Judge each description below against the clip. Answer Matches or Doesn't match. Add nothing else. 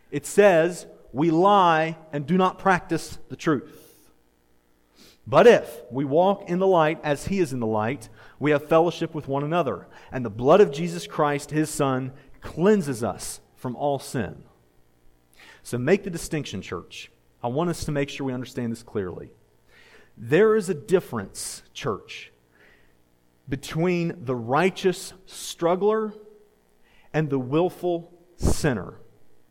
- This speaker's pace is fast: Doesn't match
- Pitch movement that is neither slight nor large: Doesn't match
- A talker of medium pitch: Matches